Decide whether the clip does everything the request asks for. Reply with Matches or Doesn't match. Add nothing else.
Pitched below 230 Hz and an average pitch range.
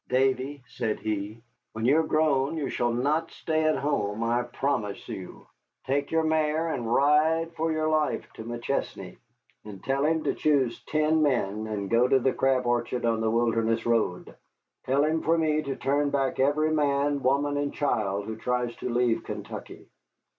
Matches